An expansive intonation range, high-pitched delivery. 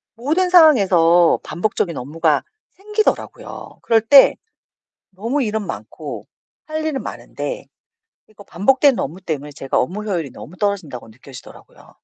Yes: wide, 8.8 semitones; high, 200 Hz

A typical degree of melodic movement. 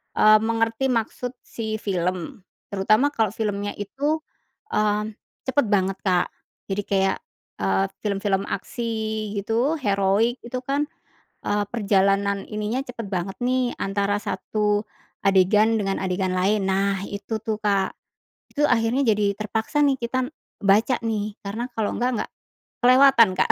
Yes: average, 3.0 semitones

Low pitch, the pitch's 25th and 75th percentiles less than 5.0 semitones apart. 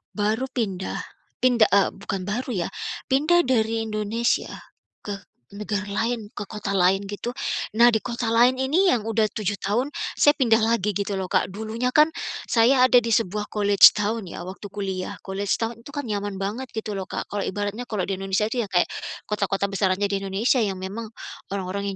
No: high, 210 Hz; average, 2.9 semitones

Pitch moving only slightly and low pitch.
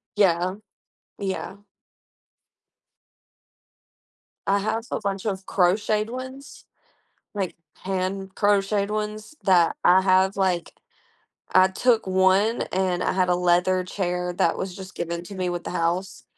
No: narrow, 2.1 semitones; high, 190 Hz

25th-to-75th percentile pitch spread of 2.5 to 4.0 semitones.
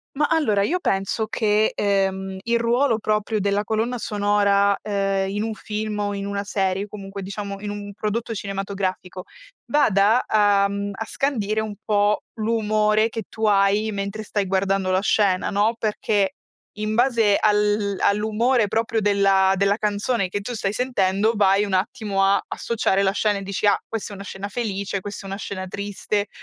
No: narrow, 1.6 semitones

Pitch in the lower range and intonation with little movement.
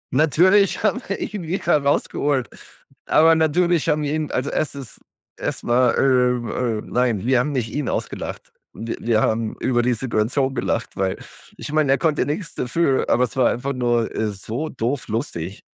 No: low, 130 Hz; average, 4.3 semitones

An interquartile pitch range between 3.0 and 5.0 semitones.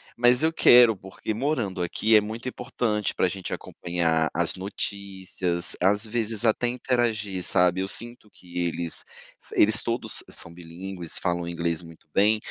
Yes: average, 4.5 semitones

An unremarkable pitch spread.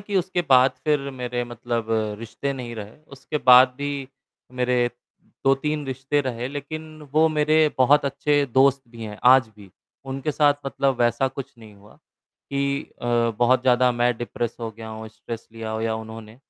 Yes: average, 3.2 semitones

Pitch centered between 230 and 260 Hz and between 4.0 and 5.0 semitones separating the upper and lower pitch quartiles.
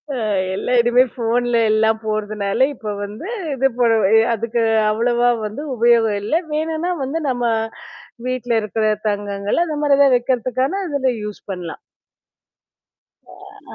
No: high, 235 Hz; average, 3.6 semitones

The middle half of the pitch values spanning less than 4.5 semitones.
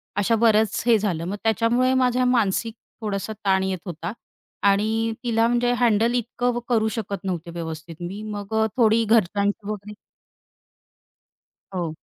Yes: average, 3.1 semitones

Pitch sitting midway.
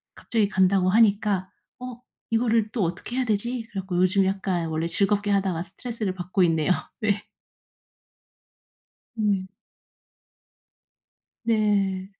No: high, 195 Hz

